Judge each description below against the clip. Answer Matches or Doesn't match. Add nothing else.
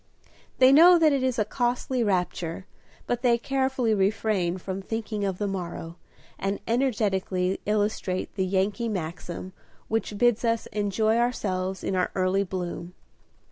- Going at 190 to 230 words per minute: Doesn't match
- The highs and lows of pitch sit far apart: Doesn't match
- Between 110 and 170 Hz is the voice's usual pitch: Doesn't match